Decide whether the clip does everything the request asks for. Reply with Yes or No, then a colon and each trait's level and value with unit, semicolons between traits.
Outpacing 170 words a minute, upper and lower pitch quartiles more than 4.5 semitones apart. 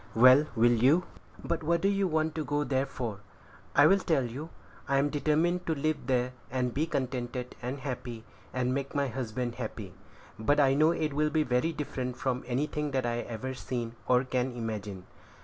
No: average, 185 wpm; average, 3.5 semitones